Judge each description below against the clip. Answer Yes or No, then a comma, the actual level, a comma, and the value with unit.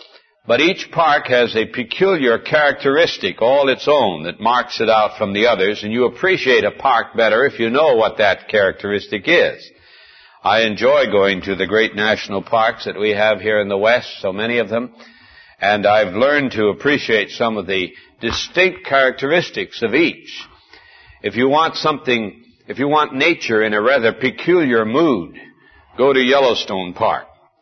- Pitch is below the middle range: Yes, low, 115 Hz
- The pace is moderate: Yes, average, 170 wpm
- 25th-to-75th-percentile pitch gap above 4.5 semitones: Yes, average, 5.1 semitones